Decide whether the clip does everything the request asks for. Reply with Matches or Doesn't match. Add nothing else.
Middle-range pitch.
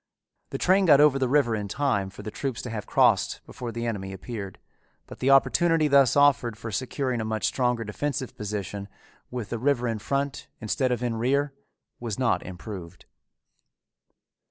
Doesn't match